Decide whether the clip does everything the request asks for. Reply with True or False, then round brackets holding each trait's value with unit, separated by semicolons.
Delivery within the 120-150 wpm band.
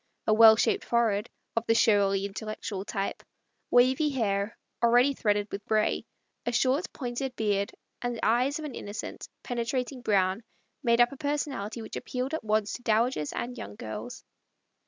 False (170 wpm)